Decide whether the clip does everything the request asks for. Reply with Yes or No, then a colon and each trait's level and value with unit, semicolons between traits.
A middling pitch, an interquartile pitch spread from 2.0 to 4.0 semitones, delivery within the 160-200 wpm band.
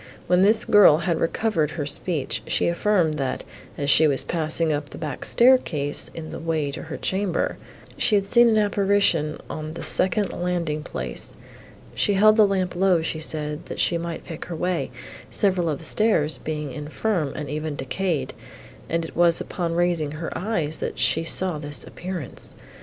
Yes: medium, 165 Hz; average, 3.7 semitones; average, 180 wpm